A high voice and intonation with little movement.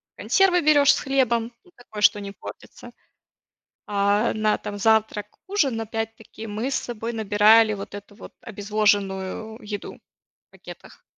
Yes: high, 220 Hz; narrow, 2.2 semitones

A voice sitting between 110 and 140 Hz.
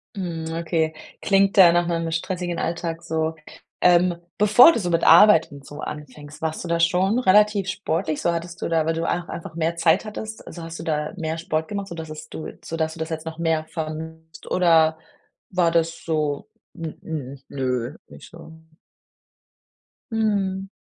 No: medium, 165 Hz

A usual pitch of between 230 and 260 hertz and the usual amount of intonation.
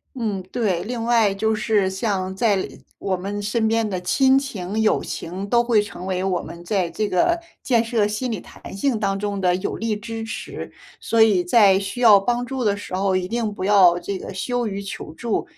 No: high, 205 Hz; average, 3.2 semitones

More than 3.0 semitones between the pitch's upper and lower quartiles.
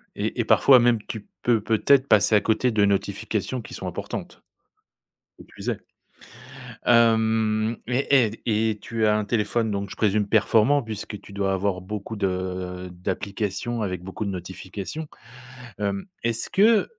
No: narrow, 2.6 semitones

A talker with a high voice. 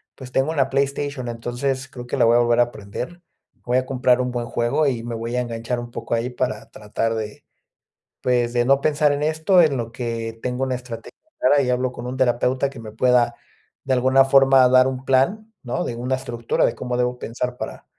No: low, 125 Hz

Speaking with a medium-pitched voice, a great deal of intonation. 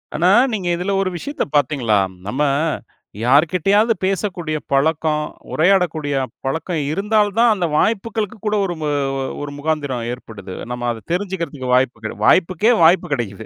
Yes: medium, 160 Hz; wide, 6.0 semitones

